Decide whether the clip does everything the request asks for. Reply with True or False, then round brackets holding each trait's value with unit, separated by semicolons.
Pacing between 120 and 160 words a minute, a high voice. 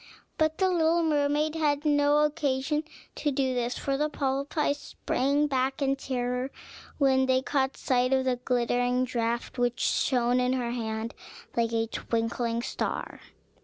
True (150 wpm; 265 Hz)